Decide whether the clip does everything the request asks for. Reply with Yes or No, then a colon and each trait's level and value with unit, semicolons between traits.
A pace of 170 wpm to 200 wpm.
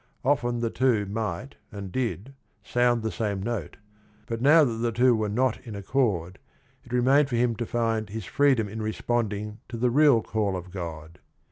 Yes: average, 180 wpm